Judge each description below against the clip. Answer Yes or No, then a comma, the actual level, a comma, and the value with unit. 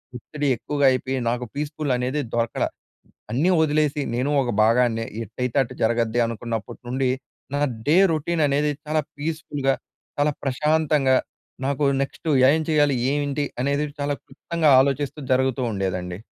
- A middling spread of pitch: Yes, average, 3.3 semitones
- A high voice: No, medium, 140 Hz